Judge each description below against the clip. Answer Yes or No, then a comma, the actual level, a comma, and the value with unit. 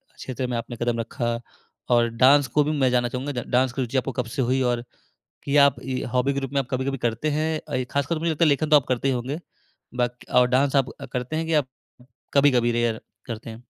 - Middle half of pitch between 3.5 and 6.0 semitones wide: No, average, 2.7 semitones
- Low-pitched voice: Yes, low, 130 Hz